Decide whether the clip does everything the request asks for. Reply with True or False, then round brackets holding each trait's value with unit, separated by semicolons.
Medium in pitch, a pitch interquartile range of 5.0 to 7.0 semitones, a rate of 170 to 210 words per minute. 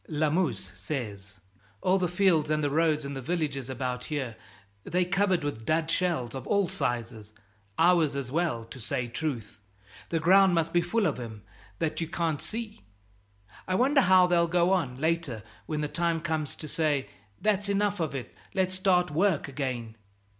True (155 Hz; 5.3 semitones; 175 wpm)